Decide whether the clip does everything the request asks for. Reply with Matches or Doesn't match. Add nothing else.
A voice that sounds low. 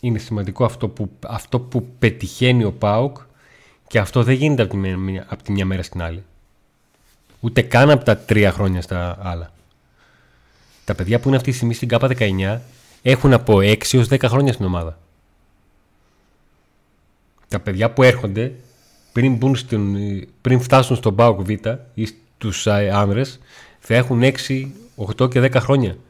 Matches